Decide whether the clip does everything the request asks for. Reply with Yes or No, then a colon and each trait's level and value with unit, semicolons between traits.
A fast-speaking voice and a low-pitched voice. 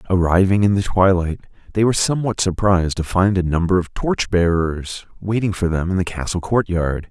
No: average, 175 wpm; very low, 95 Hz